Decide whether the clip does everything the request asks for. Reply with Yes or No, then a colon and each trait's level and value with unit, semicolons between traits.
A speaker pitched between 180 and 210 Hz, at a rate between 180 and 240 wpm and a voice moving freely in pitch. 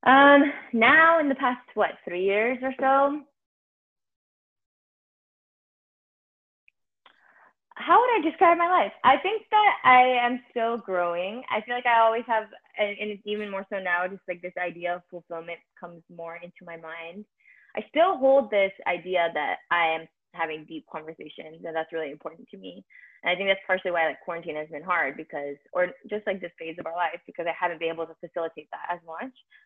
Yes: medium, 185 Hz; average, 190 wpm; wide, 6.8 semitones